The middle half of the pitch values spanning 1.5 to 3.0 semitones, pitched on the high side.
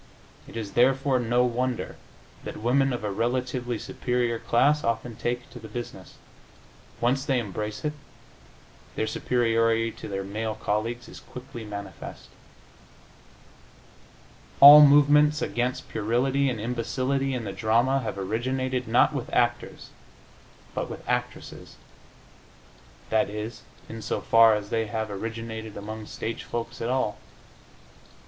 No: narrow, 2.6 semitones; low, 120 Hz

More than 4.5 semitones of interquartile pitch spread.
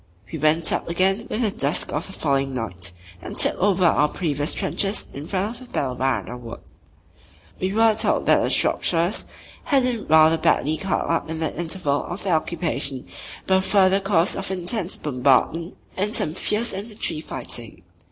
Yes: average, 5.1 semitones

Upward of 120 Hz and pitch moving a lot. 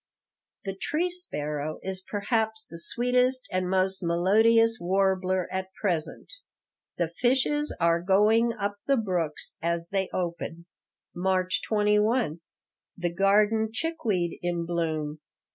No: high, 190 Hz; average, 4.5 semitones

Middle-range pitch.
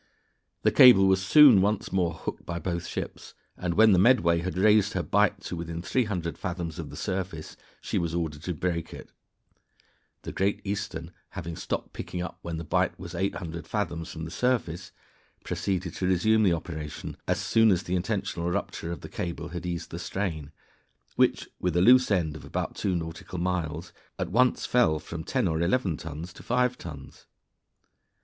No: very low, 90 Hz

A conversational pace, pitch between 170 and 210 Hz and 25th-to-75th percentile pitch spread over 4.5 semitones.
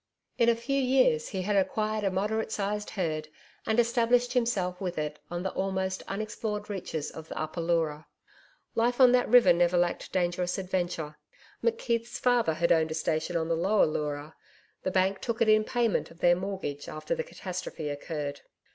Yes: average, 180 wpm; high, 190 Hz; average, 5.1 semitones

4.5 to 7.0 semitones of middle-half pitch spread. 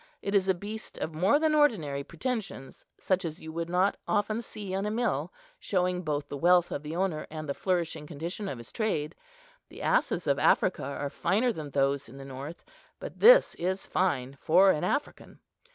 Yes: average, 5.1 semitones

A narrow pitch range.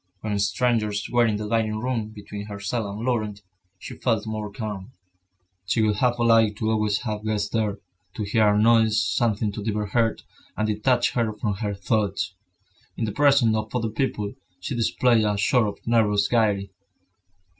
Yes: narrow, 1.9 semitones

